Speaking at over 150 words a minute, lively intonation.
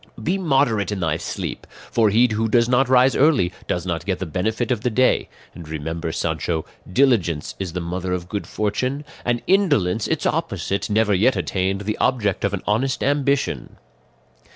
Yes: average, 175 wpm; wide, 5.8 semitones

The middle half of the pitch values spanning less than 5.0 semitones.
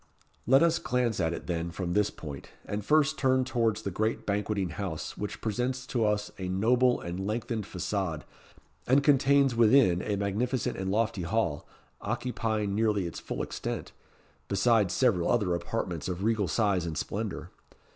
Yes: average, 4.4 semitones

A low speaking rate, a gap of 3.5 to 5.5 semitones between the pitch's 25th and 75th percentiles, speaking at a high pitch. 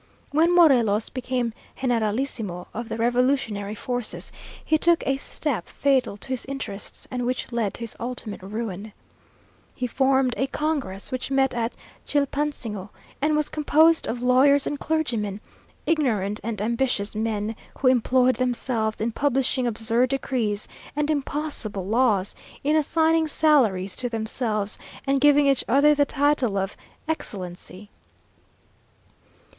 Yes: slow, 130 wpm; average, 4.5 semitones; very high, 250 Hz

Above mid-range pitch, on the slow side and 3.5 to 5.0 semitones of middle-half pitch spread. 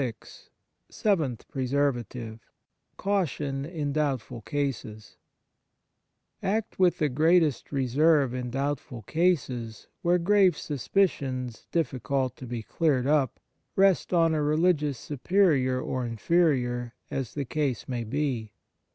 No: medium, 140 Hz; slow, 115 wpm; average, 4.7 semitones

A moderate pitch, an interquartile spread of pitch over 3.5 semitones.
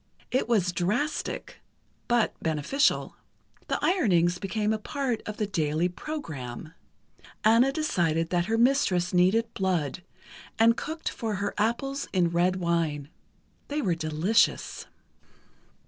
No: high, 195 Hz; wide, 5.5 semitones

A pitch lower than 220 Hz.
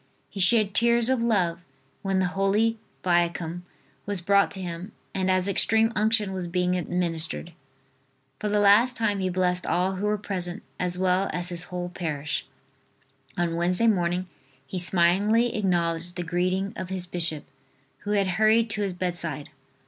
Yes: medium, 185 Hz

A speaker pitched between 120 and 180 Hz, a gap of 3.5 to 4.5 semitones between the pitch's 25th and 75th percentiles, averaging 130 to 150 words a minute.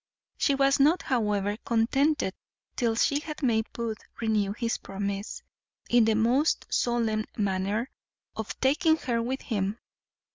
No: high, 230 Hz; average, 4.0 semitones; slow, 135 wpm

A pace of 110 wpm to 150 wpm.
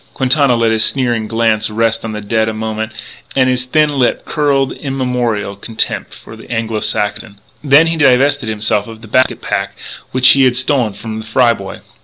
No: average, 190 wpm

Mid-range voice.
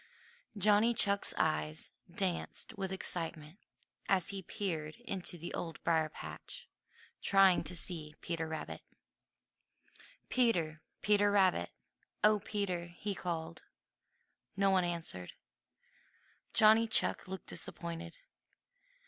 Yes: medium, 180 Hz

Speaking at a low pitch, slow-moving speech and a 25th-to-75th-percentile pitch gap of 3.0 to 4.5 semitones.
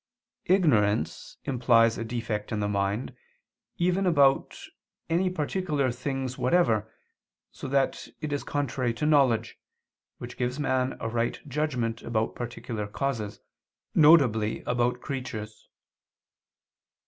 Yes: low, 125 Hz; slow, 110 wpm; average, 4.1 semitones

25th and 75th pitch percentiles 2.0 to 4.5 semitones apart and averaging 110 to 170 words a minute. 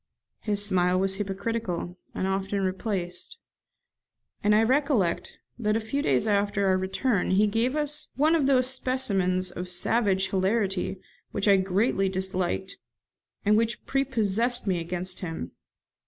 Yes: average, 3.6 semitones; average, 140 wpm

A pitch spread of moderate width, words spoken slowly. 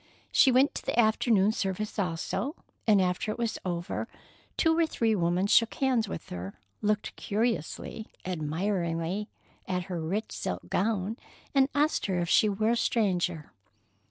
No: average, 4.4 semitones; average, 155 wpm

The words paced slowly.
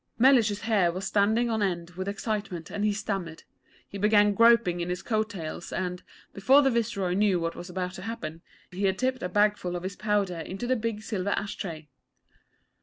No: average, 195 wpm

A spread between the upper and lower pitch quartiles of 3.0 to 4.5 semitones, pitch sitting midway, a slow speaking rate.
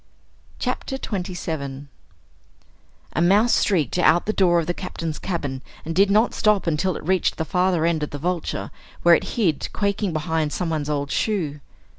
No: average, 3.7 semitones; medium, 170 Hz; average, 165 wpm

